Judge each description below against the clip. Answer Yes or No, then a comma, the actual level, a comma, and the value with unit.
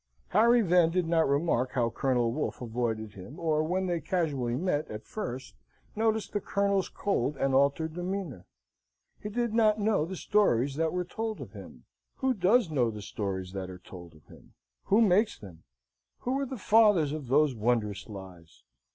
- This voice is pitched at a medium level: Yes, medium, 155 Hz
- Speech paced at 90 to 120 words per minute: No, average, 175 wpm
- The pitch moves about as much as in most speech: No, wide, 9.0 semitones